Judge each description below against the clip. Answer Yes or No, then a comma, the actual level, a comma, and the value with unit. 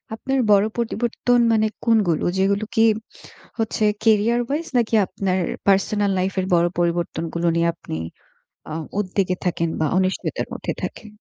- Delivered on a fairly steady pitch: No, average, 3.8 semitones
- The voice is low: No, high, 200 Hz